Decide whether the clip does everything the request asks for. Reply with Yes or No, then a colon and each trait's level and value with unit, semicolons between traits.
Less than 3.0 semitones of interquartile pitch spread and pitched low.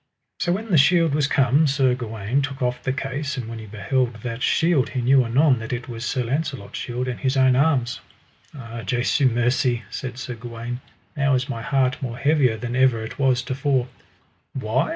Yes: narrow, 2.5 semitones; low, 130 Hz